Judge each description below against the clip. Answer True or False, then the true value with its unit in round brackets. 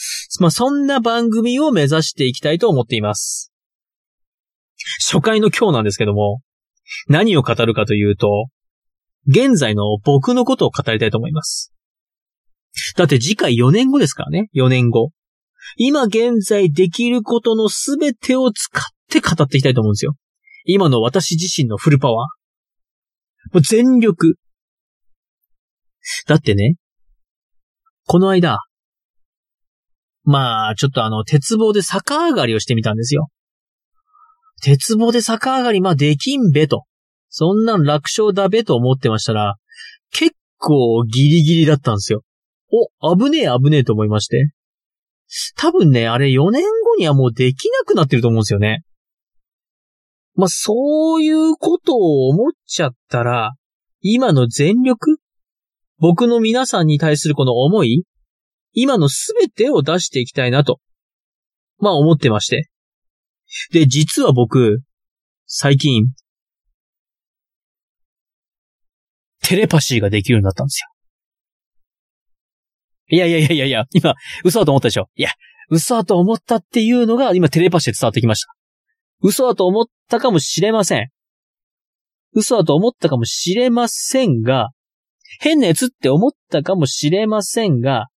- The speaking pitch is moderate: True (160 Hz)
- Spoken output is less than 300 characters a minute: True (275 characters per minute)